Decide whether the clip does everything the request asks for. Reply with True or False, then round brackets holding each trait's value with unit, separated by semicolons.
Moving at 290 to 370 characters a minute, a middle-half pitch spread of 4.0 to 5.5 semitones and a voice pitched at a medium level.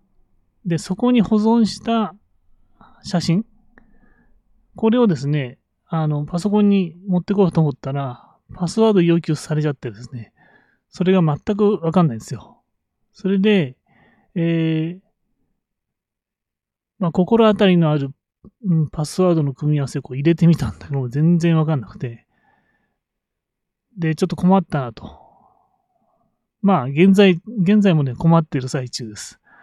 False (280 characters per minute; 5.2 semitones; 170 Hz)